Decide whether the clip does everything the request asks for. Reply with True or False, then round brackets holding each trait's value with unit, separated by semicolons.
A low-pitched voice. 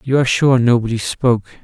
True (120 Hz)